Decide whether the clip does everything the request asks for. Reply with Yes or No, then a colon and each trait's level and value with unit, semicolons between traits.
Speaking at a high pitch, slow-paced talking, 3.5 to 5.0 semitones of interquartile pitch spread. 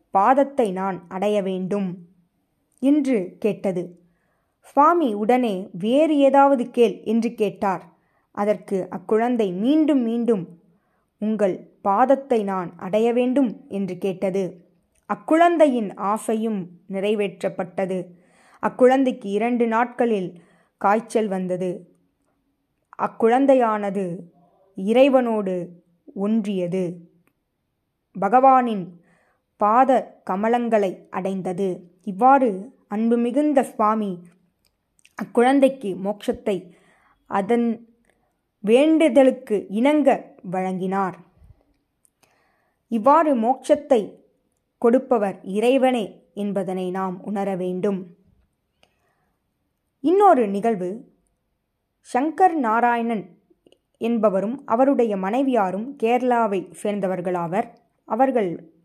Yes: high, 210 Hz; slow, 70 wpm; average, 4.5 semitones